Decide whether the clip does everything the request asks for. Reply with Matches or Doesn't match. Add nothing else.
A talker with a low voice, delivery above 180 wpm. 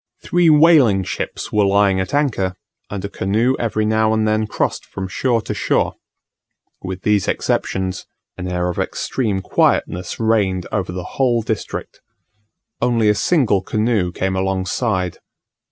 Doesn't match